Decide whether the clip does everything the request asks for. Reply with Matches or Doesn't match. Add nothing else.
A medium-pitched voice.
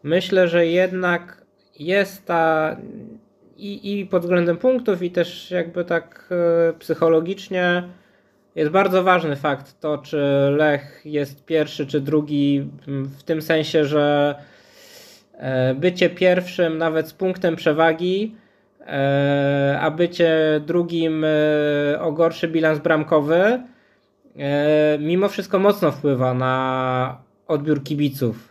Matches